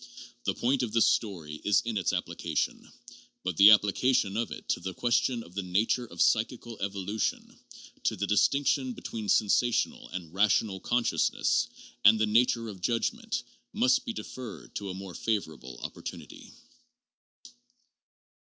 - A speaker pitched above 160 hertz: No, low, 110 Hz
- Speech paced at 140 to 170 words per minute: Yes, average, 145 wpm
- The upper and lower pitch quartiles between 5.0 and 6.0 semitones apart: No, average, 3.8 semitones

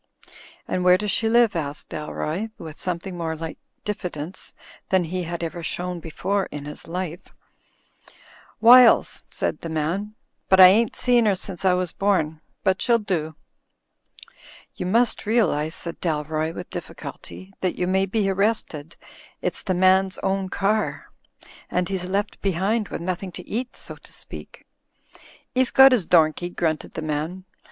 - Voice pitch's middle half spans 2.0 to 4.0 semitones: Yes, average, 3.5 semitones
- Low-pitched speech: No, medium, 185 Hz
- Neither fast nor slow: Yes, average, 160 wpm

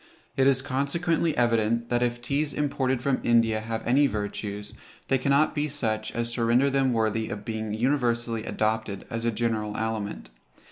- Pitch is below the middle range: Yes, low, 120 Hz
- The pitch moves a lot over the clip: No, average, 3.5 semitones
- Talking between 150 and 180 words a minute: Yes, average, 170 wpm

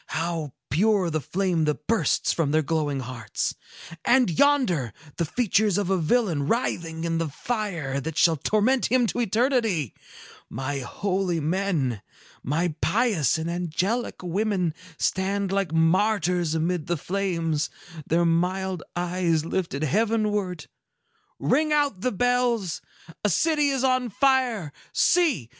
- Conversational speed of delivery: No, slow, 130 wpm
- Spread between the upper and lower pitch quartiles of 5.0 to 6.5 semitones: Yes, average, 5.3 semitones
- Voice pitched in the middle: Yes, medium, 180 Hz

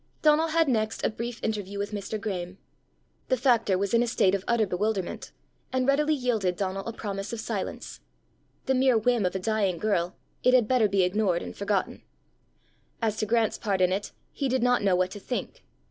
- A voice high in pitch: Yes, high, 215 Hz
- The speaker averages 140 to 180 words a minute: No, average, 200 wpm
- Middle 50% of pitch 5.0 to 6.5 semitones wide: No, average, 4.0 semitones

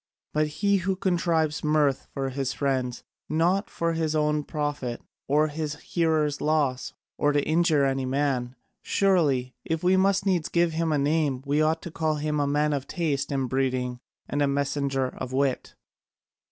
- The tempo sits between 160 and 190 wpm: Yes, average, 170 wpm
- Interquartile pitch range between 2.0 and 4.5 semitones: Yes, average, 2.9 semitones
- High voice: No, medium, 150 Hz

